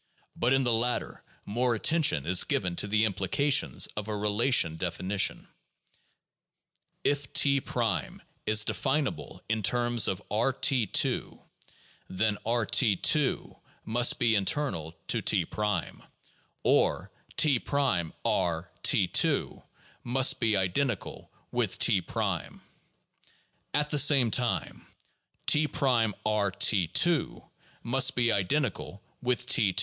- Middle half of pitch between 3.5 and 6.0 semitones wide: Yes, average, 4.9 semitones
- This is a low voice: Yes, low, 115 Hz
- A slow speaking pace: Yes, slow, 115 wpm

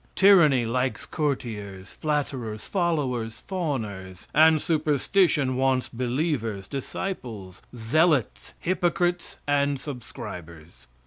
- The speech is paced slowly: Yes, slow, 80 wpm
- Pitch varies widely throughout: Yes, wide, 5.9 semitones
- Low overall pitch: Yes, low, 130 Hz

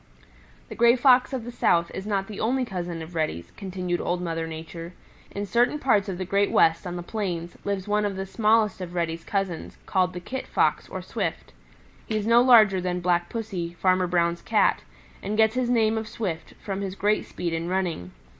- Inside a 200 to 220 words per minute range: Yes, fast, 205 wpm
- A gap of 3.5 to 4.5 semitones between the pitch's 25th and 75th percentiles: Yes, average, 3.9 semitones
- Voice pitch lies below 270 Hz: Yes, high, 190 Hz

